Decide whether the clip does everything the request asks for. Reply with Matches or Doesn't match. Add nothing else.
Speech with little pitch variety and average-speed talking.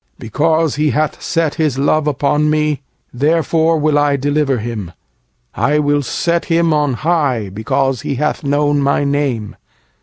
Matches